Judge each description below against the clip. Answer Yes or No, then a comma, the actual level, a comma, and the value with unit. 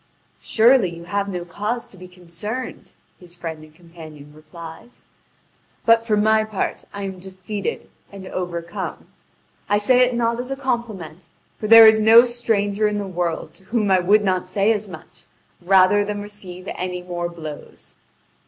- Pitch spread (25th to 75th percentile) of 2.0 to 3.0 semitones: No, average, 3.7 semitones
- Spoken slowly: No, average, 165 wpm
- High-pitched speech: Yes, high, 195 Hz